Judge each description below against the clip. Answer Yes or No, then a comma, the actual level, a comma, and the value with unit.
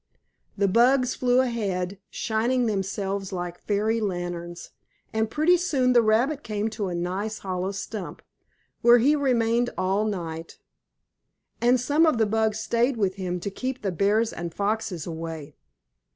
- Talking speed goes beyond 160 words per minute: No, average, 150 wpm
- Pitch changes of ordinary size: Yes, average, 4.3 semitones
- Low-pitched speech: No, high, 215 Hz